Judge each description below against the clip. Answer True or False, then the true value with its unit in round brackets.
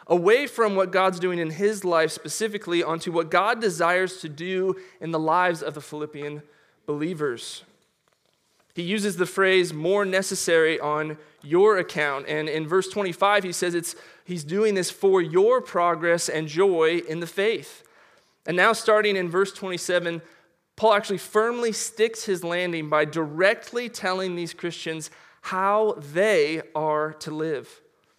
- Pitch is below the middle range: False (180 Hz)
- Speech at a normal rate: True (150 wpm)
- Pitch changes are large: False (4.0 semitones)